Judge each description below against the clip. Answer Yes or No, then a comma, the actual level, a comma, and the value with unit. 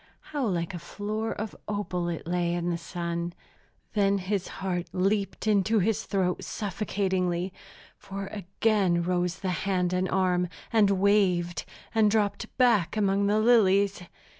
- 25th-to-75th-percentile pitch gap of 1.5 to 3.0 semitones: Yes, narrow, 2.6 semitones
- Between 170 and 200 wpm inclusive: No, average, 140 wpm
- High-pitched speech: Yes, high, 195 Hz